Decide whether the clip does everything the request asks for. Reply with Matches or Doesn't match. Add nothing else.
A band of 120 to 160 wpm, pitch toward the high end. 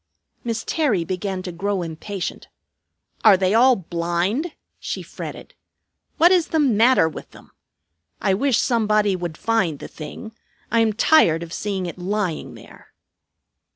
Matches